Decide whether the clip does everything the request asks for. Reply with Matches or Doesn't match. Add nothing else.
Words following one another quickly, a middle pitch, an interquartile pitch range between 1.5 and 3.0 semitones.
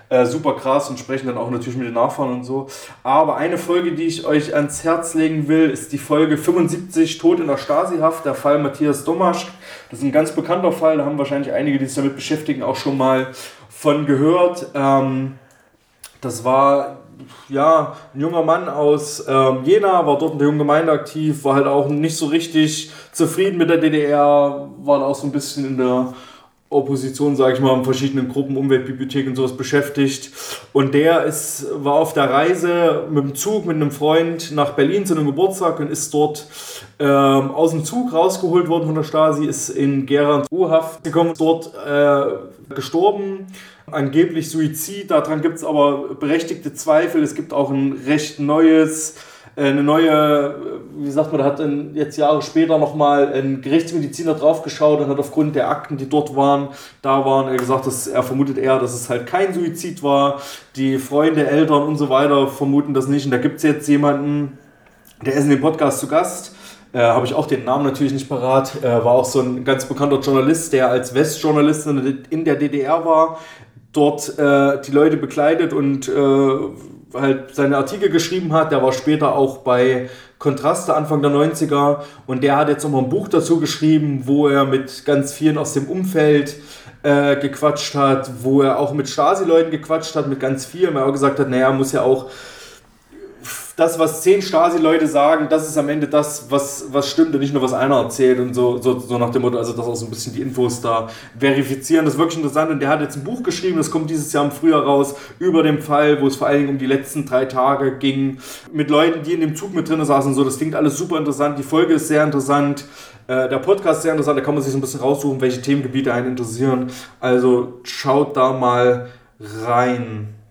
Matches